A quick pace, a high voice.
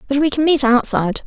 Yes: fast, 240 wpm; very high, 270 Hz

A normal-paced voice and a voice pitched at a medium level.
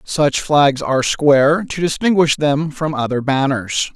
Yes: average, 150 wpm; medium, 145 Hz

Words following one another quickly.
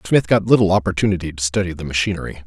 No: average, 195 wpm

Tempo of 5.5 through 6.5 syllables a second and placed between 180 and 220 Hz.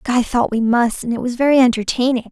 No: 5.9 syllables/s; high, 240 Hz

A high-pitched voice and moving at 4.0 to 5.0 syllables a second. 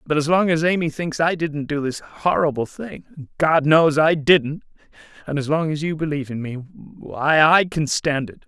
No: medium, 150 Hz; 4.7 syllables/s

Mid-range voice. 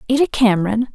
No: high, 230 Hz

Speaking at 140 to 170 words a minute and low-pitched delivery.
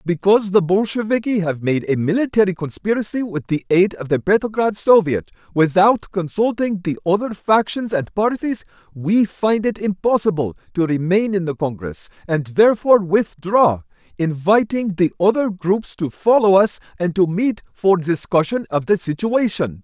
No: average, 150 wpm; high, 190 Hz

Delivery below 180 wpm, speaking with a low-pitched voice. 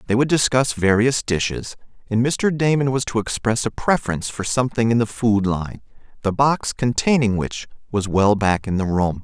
No: average, 190 wpm; low, 115 Hz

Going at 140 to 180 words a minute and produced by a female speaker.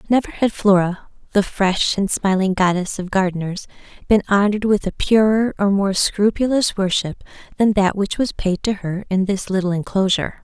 Yes: average, 170 wpm; female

